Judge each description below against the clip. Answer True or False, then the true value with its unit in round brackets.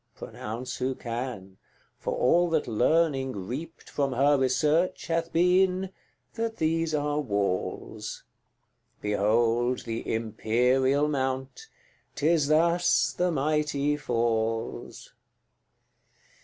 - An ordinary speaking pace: False (95 wpm)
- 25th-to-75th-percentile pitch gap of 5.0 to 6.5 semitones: True (5.6 semitones)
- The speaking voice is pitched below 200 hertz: True (135 Hz)